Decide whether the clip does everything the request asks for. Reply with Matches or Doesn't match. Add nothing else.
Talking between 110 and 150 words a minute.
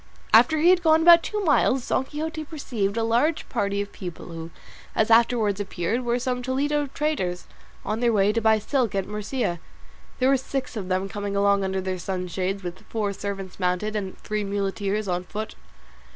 Doesn't match